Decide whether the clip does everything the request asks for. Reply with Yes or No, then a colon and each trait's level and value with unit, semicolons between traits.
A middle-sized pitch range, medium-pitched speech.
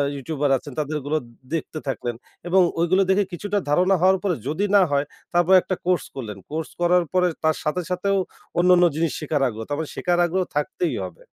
Yes: average, 3.8 semitones; medium, 170 Hz